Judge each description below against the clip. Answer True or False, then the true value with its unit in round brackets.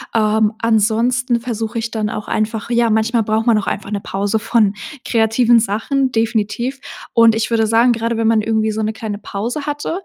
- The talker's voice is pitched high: True (225 Hz)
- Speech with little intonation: True (1.5 semitones)